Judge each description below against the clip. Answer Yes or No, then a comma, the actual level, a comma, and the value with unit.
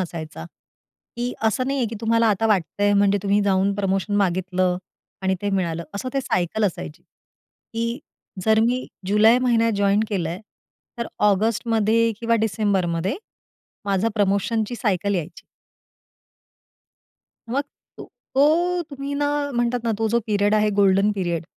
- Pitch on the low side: No, high, 205 Hz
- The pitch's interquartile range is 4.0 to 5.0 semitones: No, average, 3.3 semitones